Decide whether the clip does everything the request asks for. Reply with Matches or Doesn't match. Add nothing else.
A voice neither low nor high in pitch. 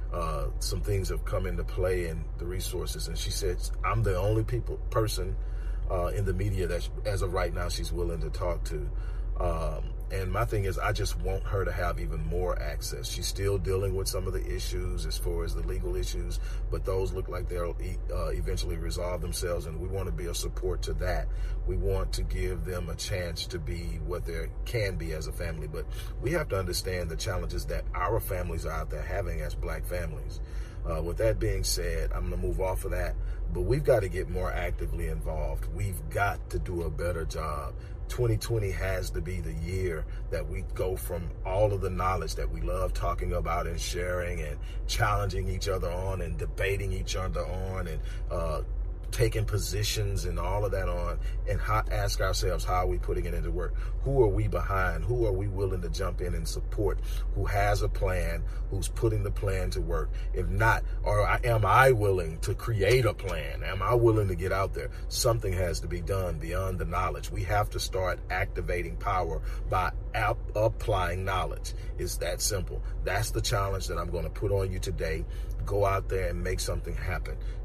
Doesn't match